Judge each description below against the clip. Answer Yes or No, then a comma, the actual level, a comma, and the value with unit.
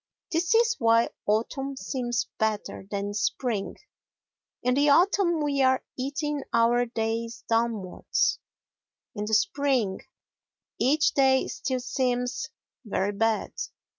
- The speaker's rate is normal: No, slow, 110 wpm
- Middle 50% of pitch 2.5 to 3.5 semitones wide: No, average, 4.0 semitones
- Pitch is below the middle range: No, high, 245 Hz